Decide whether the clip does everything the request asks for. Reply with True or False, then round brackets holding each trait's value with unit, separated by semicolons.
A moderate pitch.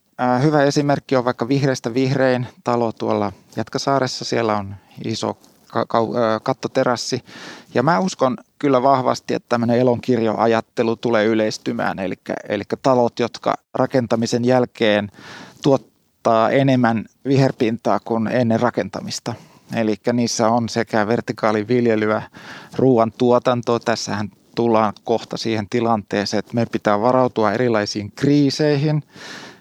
False (115 Hz)